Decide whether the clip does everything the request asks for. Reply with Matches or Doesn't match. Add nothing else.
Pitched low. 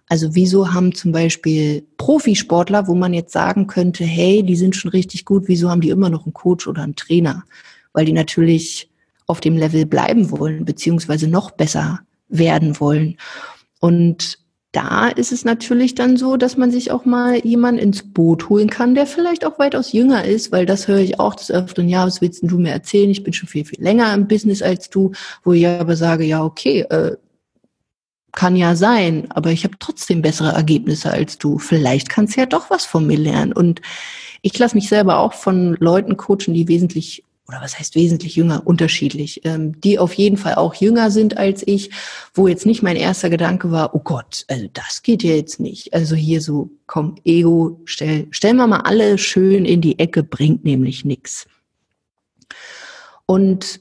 Doesn't match